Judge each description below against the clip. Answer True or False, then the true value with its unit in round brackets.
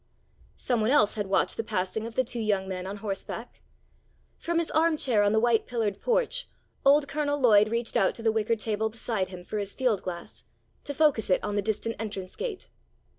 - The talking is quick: True (210 wpm)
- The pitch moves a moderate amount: True (4.1 semitones)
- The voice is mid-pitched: False (220 Hz)